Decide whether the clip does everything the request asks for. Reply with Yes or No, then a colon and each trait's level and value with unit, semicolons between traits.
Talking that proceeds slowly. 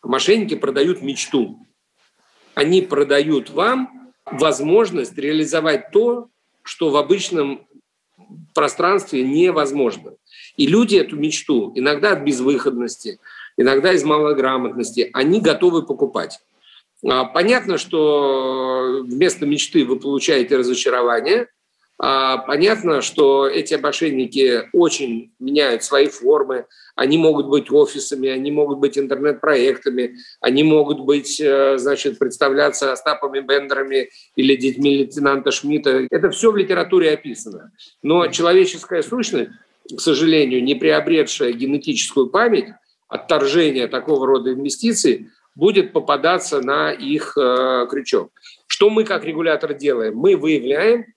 Yes: slow, 105 wpm